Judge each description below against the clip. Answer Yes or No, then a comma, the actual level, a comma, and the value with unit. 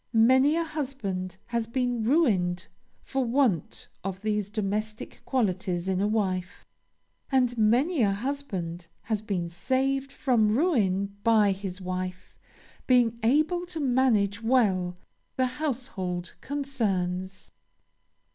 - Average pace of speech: No, slow, 115 wpm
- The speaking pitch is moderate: No, high, 220 Hz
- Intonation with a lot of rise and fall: Yes, wide, 5.7 semitones